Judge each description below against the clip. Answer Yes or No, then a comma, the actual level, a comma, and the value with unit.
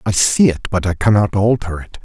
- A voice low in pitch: Yes, low, 100 Hz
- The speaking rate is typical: No, fast, 235 wpm